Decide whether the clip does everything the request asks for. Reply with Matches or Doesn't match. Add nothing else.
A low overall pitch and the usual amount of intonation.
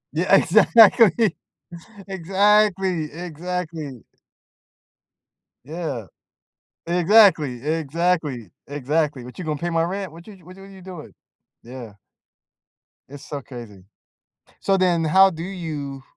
Doesn't match